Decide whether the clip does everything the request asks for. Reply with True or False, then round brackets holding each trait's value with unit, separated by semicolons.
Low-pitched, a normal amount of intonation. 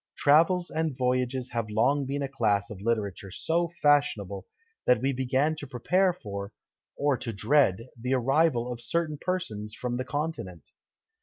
True (130 Hz; 4.8 semitones)